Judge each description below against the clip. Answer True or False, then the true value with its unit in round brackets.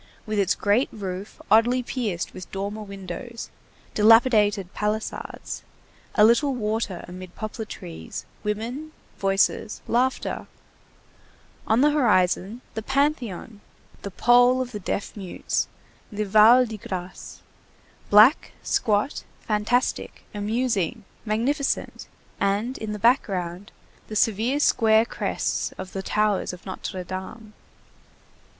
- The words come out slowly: True (115 wpm)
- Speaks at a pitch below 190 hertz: False (215 Hz)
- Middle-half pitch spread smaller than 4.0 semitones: True (3.5 semitones)